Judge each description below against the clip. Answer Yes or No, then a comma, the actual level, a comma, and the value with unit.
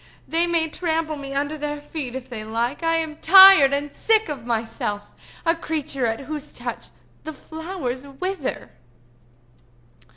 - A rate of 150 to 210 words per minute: No, average, 140 wpm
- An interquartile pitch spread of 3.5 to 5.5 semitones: Yes, average, 3.8 semitones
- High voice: Yes, very high, 295 Hz